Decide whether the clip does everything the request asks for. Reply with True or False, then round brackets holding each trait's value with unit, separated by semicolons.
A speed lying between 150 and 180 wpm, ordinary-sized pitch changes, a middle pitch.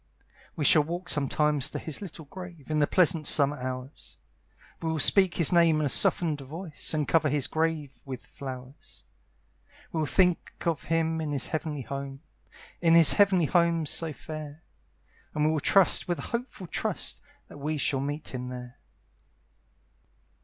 True (165 wpm; 3.0 semitones; 155 Hz)